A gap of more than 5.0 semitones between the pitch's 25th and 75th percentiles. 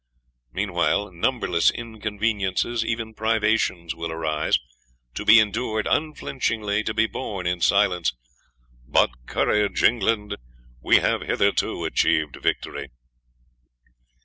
No: average, 3.9 semitones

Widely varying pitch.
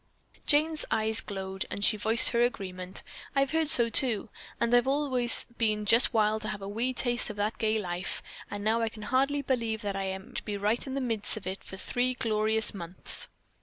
No: average, 3.1 semitones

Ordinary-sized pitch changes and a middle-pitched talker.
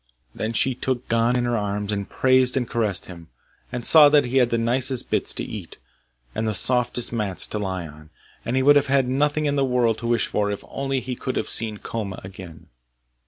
No: average, 4.0 semitones; low, 120 Hz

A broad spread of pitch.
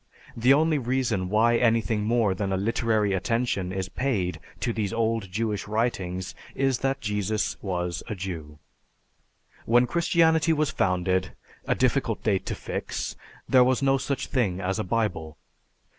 No: average, 4.8 semitones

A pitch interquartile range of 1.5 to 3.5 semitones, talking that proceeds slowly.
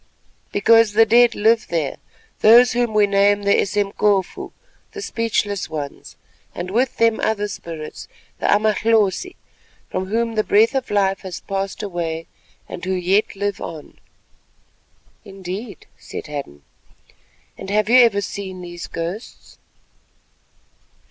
Yes: average, 3.2 semitones; slow, 130 wpm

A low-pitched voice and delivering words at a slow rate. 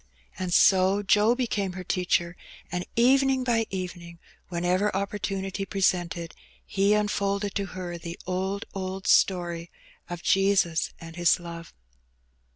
No: high, 190 Hz; slow, 125 wpm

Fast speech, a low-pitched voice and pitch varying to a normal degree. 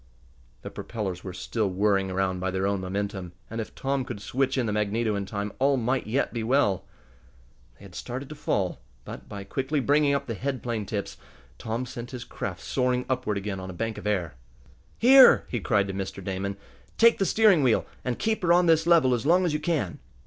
No: fast, 215 wpm; low, 115 Hz; wide, 5.7 semitones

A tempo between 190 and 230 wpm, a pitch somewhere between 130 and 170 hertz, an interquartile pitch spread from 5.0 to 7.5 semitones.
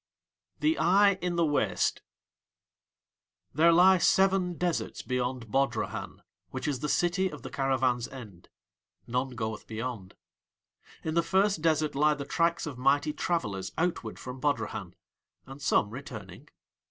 No: slow, 135 wpm; medium, 140 Hz; wide, 5.5 semitones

